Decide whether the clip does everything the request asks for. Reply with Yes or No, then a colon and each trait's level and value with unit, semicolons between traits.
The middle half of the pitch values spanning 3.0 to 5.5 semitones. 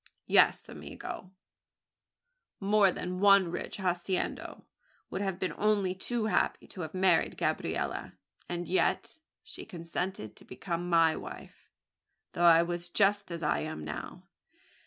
No: narrow, 2.5 semitones